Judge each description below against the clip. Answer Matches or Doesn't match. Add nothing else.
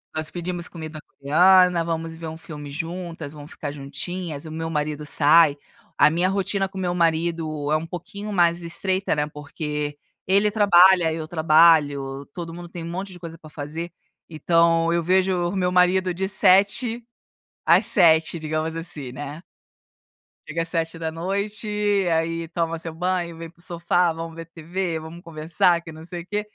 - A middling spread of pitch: Doesn't match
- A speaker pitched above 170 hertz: Doesn't match